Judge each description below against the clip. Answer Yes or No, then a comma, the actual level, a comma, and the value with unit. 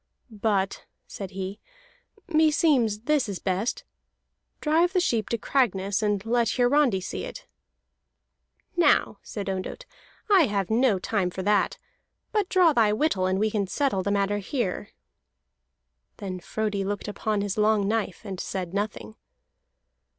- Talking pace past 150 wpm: No, average, 140 wpm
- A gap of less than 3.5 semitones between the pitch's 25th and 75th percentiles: No, average, 4.6 semitones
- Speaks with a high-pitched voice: Yes, high, 210 Hz